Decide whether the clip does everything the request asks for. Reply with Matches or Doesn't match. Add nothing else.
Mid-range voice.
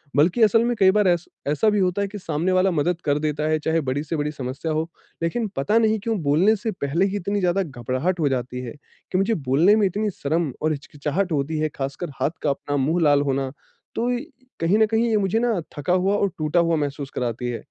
Matches